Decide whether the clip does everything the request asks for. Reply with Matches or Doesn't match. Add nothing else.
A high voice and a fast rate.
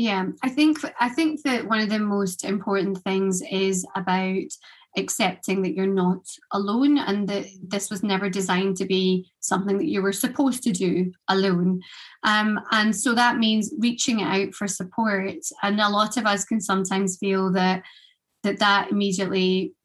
Doesn't match